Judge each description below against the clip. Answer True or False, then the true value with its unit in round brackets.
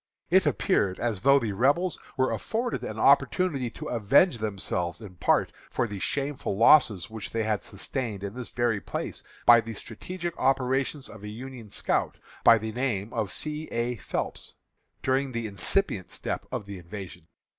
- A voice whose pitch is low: True (115 Hz)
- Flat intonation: False (4.7 semitones)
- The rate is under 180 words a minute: True (165 wpm)